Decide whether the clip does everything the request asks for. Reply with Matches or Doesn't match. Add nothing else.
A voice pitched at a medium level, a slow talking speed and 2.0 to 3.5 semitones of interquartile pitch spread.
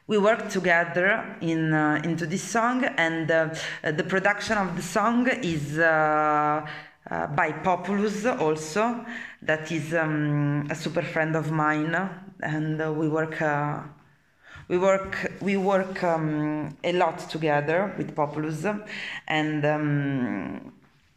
Doesn't match